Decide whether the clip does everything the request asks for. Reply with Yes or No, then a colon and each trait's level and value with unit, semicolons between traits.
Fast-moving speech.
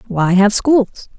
No: average, 150 wpm